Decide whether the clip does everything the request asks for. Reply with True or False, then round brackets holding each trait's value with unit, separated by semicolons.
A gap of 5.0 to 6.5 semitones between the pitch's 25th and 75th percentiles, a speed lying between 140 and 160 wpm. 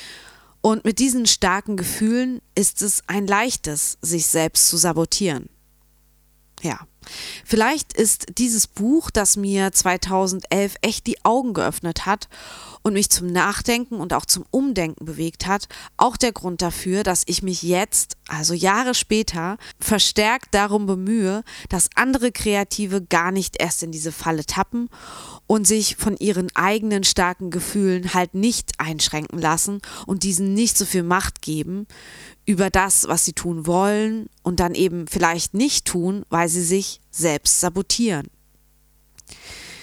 False (3.7 semitones; 145 wpm)